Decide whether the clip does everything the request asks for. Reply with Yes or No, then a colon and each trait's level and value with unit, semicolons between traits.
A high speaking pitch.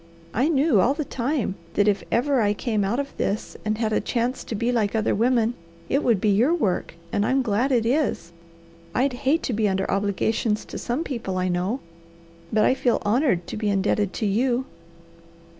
Yes: high, 225 Hz